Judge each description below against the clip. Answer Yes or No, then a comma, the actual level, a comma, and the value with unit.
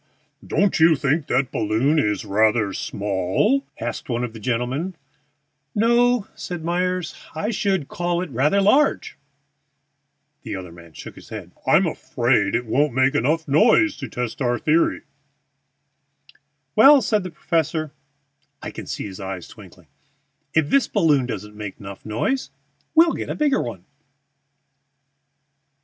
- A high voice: No, medium, 145 Hz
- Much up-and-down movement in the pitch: Yes, wide, 8.9 semitones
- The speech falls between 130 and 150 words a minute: Yes, average, 140 wpm